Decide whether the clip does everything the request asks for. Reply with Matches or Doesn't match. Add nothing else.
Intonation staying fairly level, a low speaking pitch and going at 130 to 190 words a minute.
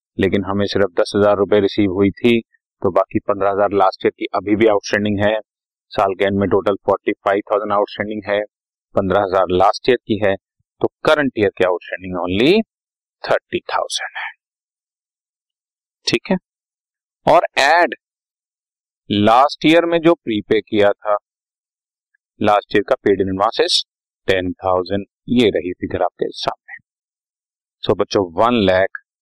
Matches